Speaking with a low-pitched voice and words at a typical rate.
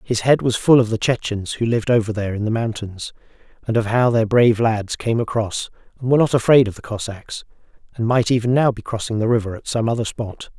No: low, 115 Hz; fast, 230 wpm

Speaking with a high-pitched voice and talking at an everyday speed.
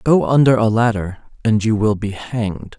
No: low, 110 Hz; average, 195 wpm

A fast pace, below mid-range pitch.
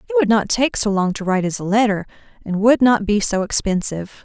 No: fast, 240 wpm; high, 215 Hz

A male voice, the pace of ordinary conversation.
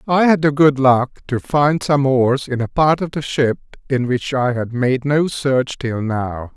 No: male; fast, 220 wpm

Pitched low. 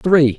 No: medium, 155 Hz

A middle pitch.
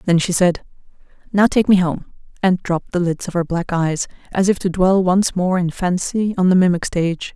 Yes: medium, 180 Hz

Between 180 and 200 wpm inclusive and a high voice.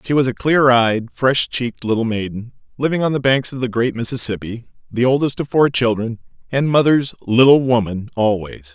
No: average, 185 wpm; low, 125 Hz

